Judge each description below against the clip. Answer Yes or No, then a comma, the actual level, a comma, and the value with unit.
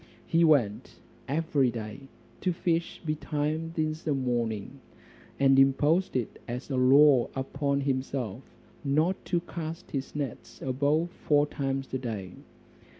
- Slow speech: Yes, slow, 130 wpm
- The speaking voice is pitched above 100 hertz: Yes, medium, 140 Hz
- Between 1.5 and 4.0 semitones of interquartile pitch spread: Yes, average, 3.1 semitones